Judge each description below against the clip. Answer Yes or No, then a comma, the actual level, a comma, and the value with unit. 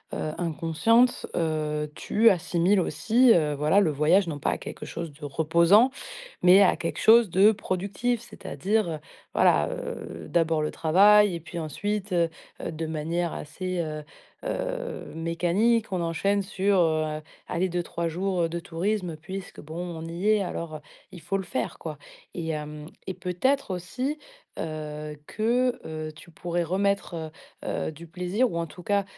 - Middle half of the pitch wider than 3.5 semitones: Yes, average, 4.1 semitones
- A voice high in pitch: No, medium, 175 Hz